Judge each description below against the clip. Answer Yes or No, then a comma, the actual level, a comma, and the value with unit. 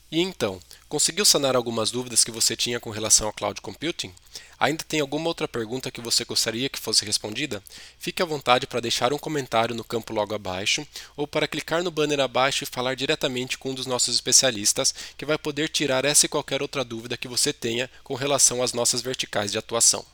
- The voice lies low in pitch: Yes, low, 125 Hz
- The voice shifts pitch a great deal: No, average, 4.3 semitones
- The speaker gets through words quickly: Yes, fast, 205 wpm